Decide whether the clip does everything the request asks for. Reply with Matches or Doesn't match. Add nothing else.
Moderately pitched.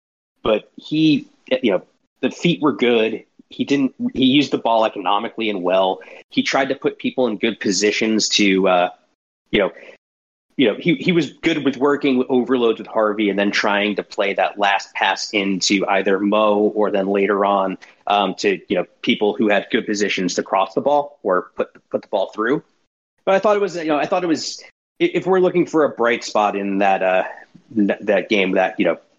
Doesn't match